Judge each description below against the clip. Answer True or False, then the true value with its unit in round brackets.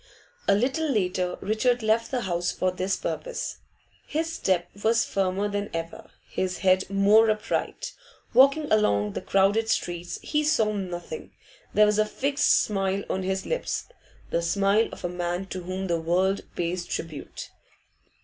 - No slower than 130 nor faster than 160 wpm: True (155 wpm)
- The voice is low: False (195 Hz)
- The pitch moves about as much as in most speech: True (3.5 semitones)